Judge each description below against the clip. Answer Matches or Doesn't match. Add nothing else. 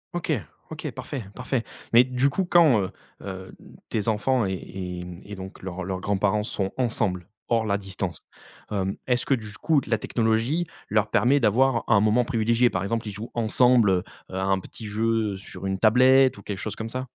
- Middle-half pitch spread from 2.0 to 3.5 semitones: Doesn't match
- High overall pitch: Doesn't match